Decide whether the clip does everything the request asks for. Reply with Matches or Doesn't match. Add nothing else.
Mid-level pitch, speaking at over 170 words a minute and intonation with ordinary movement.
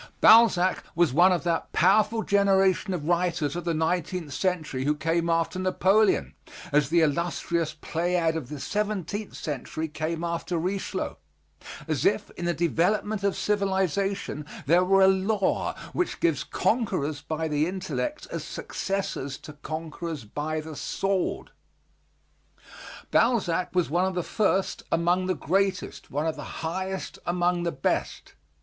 Doesn't match